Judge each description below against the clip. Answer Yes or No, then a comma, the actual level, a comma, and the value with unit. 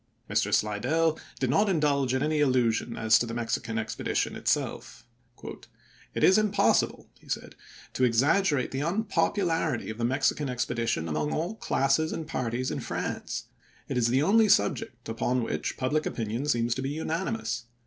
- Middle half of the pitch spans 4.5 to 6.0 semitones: Yes, wide, 5.4 semitones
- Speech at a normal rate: Yes, average, 160 wpm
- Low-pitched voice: Yes, low, 130 Hz